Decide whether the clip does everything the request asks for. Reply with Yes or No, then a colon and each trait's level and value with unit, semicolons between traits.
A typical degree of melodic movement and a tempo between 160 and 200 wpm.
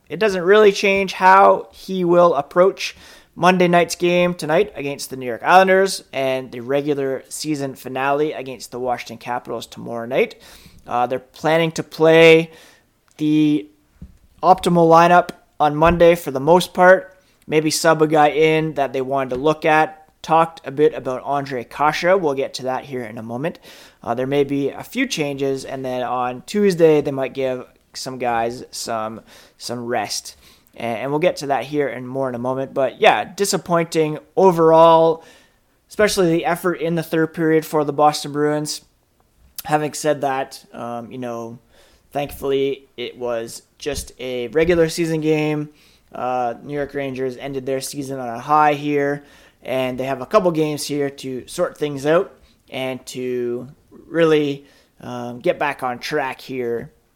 Yes: average, 3.9 semitones; average, 165 wpm